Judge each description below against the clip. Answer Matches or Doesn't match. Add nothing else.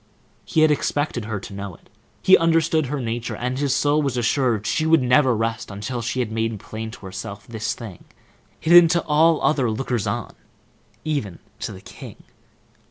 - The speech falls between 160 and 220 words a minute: Matches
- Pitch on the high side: Doesn't match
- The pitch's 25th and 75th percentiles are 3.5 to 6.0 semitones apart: Matches